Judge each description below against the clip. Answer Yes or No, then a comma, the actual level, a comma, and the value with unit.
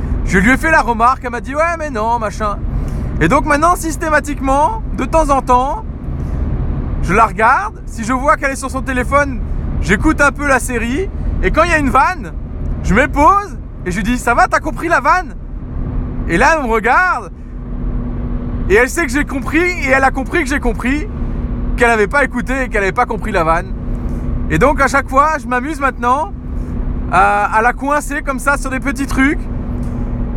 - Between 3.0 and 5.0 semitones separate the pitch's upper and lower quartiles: Yes, average, 3.8 semitones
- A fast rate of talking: No, average, 205 wpm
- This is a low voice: No, very high, 265 Hz